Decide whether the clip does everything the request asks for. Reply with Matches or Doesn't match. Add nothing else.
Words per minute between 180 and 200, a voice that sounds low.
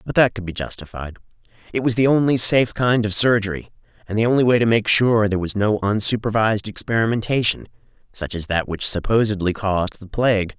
Matches